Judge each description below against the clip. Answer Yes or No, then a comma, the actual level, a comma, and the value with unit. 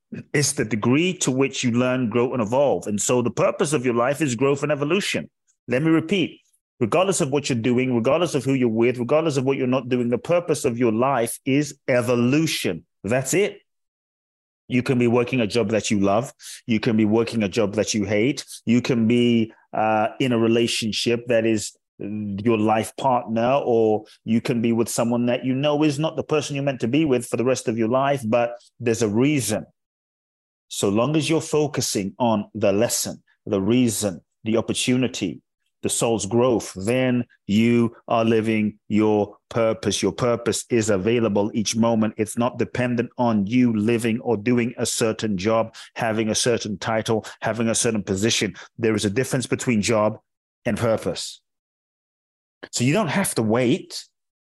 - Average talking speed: Yes, average, 185 wpm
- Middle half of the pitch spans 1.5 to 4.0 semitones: Yes, average, 2.7 semitones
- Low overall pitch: Yes, low, 120 Hz